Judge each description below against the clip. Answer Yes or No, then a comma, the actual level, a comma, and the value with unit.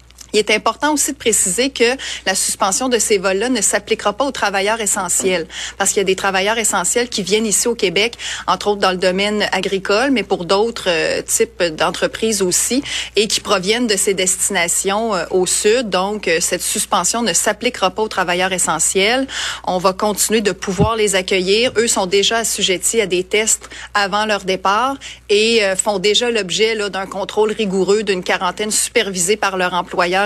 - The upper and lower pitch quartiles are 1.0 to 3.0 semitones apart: Yes, narrow, 2.6 semitones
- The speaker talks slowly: No, average, 185 wpm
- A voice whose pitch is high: Yes, high, 205 Hz